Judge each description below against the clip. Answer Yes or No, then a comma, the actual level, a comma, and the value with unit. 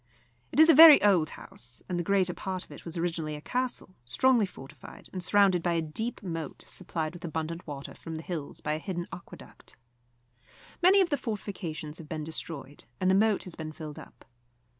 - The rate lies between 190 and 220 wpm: Yes, average, 200 wpm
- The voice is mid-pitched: Yes, medium, 175 Hz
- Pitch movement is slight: No, average, 4.3 semitones